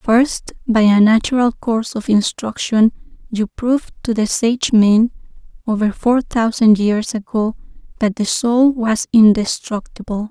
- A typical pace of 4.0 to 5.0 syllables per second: Yes, 4.3 syllables/s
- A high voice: Yes, high, 225 Hz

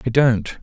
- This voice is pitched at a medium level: No, low, 120 Hz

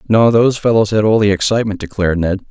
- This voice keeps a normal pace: No, fast, 215 wpm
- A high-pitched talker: No, low, 105 Hz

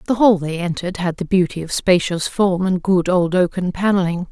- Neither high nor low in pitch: Yes, medium, 180 Hz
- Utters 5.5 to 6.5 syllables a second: No, 5.3 syllables/s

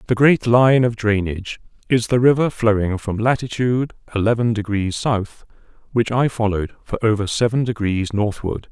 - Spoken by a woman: No, male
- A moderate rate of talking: Yes, average, 150 wpm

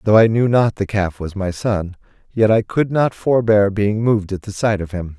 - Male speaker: Yes, male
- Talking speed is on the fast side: Yes, fast, 245 wpm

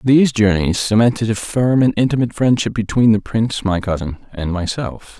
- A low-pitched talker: Yes, low, 110 Hz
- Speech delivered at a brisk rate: No, average, 175 wpm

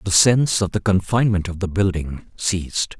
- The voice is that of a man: Yes, male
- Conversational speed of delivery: Yes, average, 180 wpm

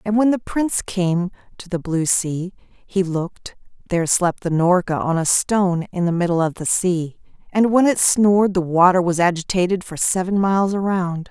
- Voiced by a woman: Yes, female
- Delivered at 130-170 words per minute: No, average, 185 wpm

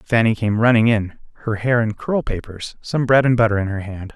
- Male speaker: Yes, male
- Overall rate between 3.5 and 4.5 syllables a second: No, 5.3 syllables/s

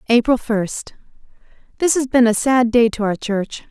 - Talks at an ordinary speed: Yes, average, 160 wpm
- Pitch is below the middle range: No, high, 235 Hz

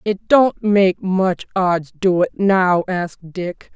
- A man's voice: No, female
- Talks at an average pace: Yes, average, 160 wpm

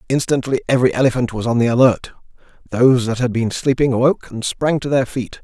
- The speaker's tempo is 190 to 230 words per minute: Yes, average, 200 wpm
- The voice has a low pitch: Yes, low, 125 Hz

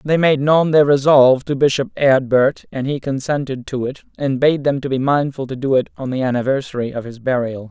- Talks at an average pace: No, fast, 220 wpm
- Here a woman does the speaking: No, male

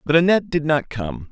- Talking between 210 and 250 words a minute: Yes, fast, 230 wpm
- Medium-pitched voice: Yes, medium, 150 Hz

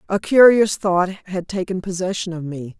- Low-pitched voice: No, medium, 185 Hz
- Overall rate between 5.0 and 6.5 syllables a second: No, 4.6 syllables/s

